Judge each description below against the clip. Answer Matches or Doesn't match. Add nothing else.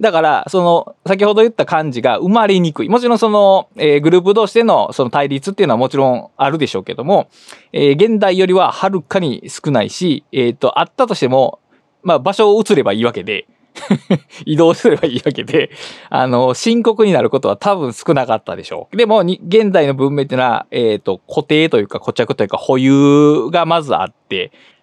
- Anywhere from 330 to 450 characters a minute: Matches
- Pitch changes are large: Matches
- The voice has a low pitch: Doesn't match